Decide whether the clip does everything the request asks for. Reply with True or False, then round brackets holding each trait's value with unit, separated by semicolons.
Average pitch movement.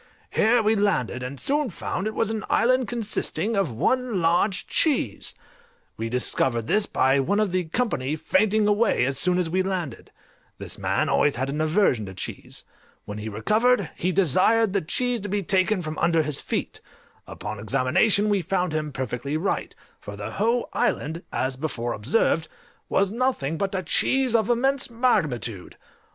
False (8.0 semitones)